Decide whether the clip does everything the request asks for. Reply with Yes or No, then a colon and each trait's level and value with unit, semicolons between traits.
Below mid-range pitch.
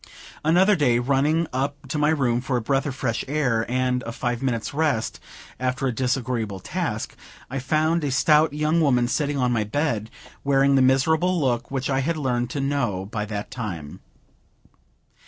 Yes: low, 130 Hz